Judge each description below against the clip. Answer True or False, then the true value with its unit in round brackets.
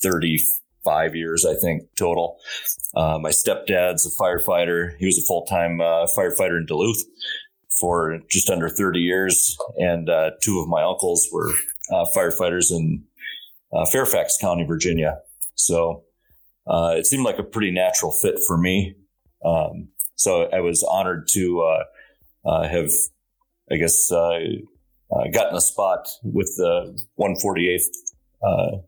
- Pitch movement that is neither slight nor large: False (2.2 semitones)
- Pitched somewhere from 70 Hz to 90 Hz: True (85 Hz)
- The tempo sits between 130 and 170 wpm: True (140 wpm)